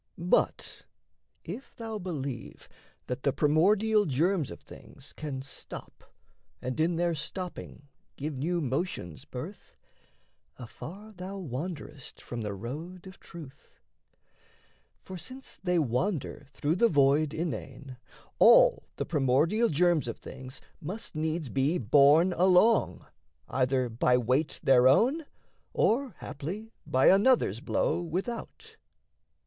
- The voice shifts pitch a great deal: Yes, wide, 5.8 semitones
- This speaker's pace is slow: Yes, slow, 120 wpm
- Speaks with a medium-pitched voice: Yes, medium, 160 Hz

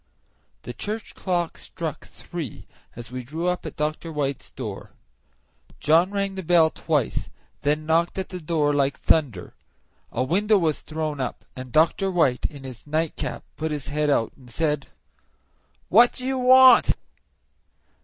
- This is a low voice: No, medium, 155 Hz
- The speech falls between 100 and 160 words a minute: Yes, average, 155 wpm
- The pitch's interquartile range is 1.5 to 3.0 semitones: No, average, 3.9 semitones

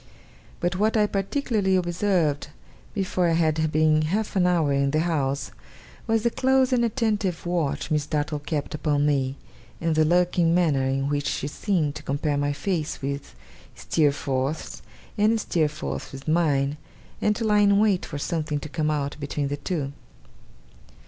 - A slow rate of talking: No, average, 160 wpm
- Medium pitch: Yes, medium, 155 Hz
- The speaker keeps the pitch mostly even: No, average, 4.7 semitones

